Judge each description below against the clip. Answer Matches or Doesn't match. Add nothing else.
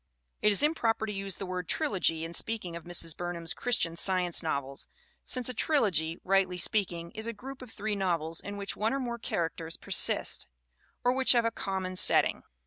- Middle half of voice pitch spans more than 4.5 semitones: Matches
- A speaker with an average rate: Matches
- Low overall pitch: Doesn't match